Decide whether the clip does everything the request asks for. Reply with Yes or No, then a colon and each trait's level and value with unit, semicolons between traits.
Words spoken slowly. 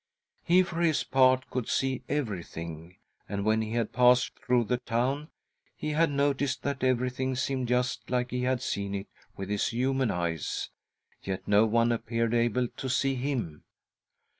No: average, 165 wpm